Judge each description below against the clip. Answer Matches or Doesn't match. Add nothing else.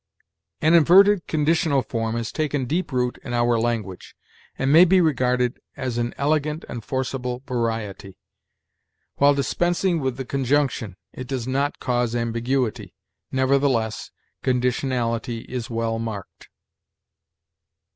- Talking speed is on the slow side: Matches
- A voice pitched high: Doesn't match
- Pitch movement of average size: Matches